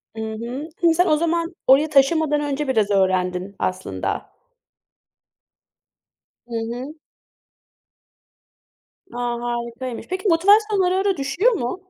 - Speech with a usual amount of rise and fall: No, wide, 6.4 semitones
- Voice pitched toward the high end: Yes, very high, 275 Hz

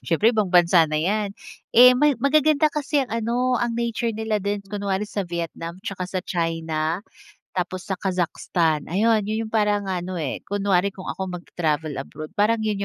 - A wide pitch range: No, average, 4.2 semitones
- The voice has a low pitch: No, high, 200 Hz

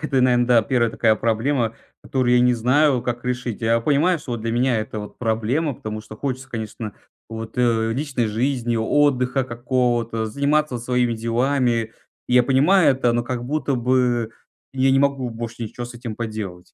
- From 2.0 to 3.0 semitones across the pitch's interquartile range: Yes, narrow, 2.4 semitones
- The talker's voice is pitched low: Yes, low, 120 Hz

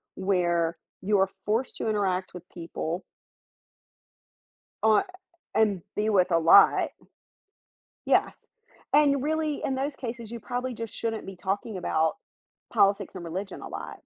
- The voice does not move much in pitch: No, average, 4.0 semitones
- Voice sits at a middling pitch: No, high, 205 Hz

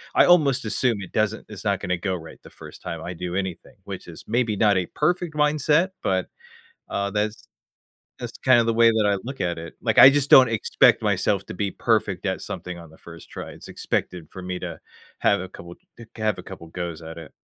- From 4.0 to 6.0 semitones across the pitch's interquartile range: Yes, average, 5.2 semitones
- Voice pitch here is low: Yes, low, 100 Hz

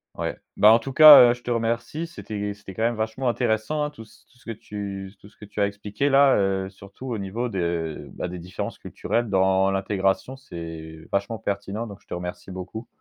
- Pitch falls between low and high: No, low, 105 Hz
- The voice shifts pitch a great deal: No, average, 3.6 semitones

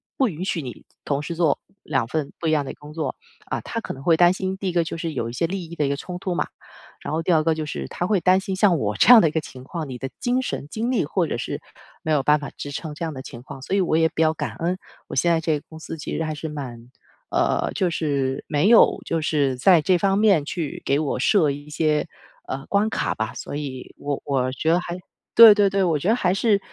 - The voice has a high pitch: No, medium, 160 Hz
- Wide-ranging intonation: No, average, 4.1 semitones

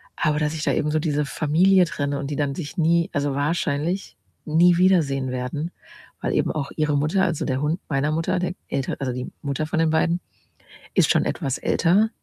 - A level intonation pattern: No, average, 3.1 semitones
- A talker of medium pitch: Yes, medium, 150 Hz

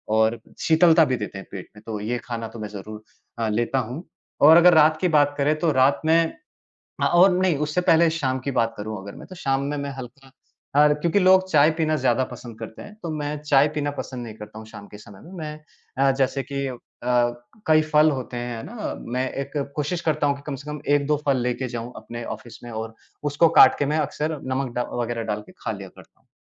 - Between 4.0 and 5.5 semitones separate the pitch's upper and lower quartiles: Yes, average, 4.4 semitones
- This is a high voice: No, low, 135 Hz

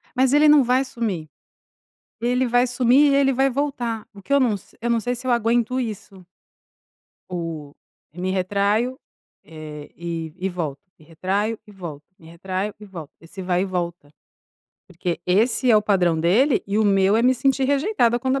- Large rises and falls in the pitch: Yes, wide, 5.9 semitones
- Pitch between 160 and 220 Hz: Yes, high, 210 Hz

